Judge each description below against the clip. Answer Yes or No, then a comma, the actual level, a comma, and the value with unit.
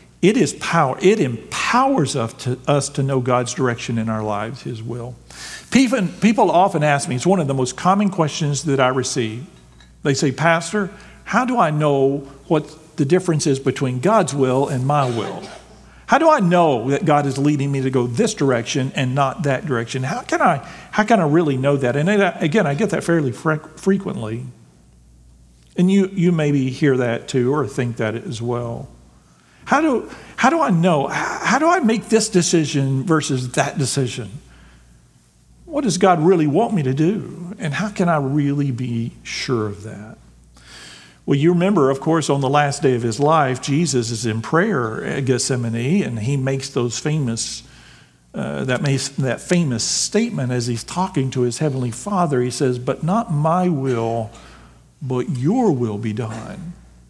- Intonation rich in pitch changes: Yes, wide, 5.7 semitones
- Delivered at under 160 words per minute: No, average, 180 wpm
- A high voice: No, medium, 140 Hz